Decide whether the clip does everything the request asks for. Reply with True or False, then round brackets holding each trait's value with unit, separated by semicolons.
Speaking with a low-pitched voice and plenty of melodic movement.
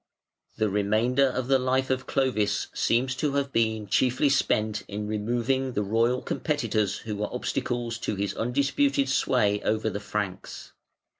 False (115 Hz; 3.8 semitones)